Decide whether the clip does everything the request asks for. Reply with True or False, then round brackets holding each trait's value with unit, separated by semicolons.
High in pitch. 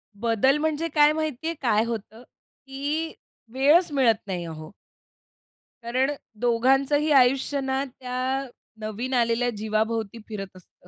True (250 Hz)